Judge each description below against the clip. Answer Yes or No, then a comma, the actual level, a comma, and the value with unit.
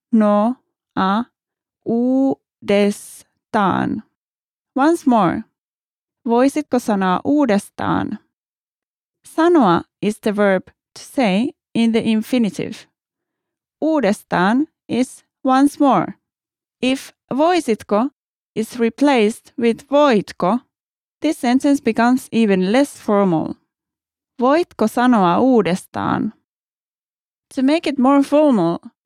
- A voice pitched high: Yes, high, 245 Hz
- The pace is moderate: No, slow, 85 wpm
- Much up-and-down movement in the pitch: No, average, 4.6 semitones